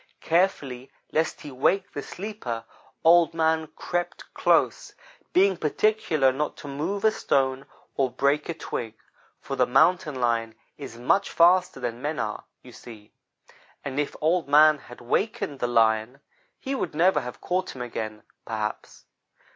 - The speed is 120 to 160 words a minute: Yes, average, 150 wpm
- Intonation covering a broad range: Yes, wide, 5.8 semitones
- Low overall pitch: No, medium, 145 Hz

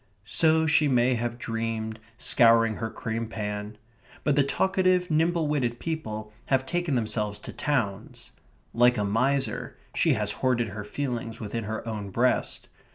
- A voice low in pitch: Yes, low, 120 Hz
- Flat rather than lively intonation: No, average, 4.5 semitones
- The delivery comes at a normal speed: Yes, average, 150 wpm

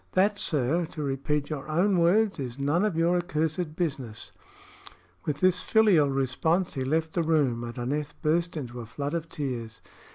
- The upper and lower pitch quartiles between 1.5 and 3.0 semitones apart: No, average, 4.0 semitones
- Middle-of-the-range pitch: Yes, medium, 155 Hz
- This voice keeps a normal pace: Yes, average, 170 wpm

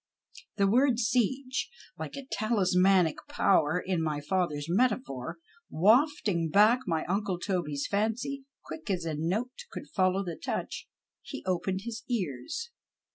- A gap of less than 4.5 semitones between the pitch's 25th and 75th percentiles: No, wide, 5.6 semitones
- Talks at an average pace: No, slow, 130 wpm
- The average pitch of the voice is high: Yes, high, 195 Hz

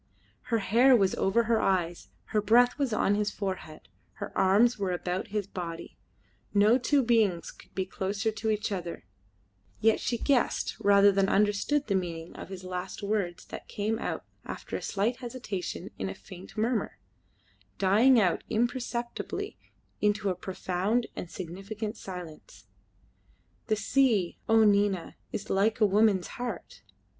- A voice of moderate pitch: No, high, 205 Hz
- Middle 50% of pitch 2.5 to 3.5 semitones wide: Yes, average, 3.2 semitones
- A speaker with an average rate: Yes, average, 150 wpm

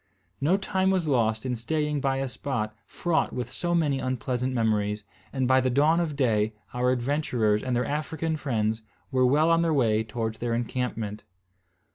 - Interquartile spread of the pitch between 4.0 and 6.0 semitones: Yes, average, 4.8 semitones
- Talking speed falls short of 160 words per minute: No, average, 175 wpm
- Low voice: Yes, low, 130 Hz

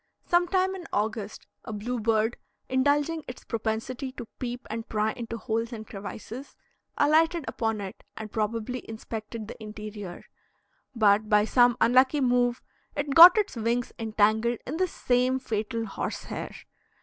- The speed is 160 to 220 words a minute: No, average, 145 wpm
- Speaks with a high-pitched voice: Yes, high, 230 Hz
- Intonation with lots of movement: No, average, 3.1 semitones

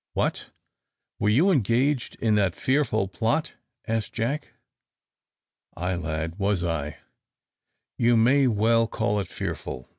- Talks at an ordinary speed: No, slow, 120 wpm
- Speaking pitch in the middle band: No, low, 110 Hz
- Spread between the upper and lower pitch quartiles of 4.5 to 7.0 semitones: Yes, average, 4.9 semitones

